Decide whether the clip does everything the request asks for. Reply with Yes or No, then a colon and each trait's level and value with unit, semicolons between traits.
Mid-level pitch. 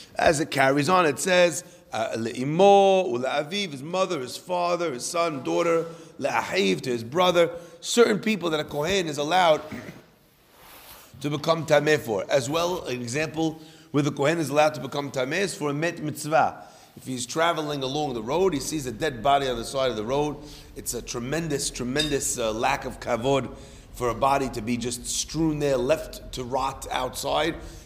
Yes: medium, 150 Hz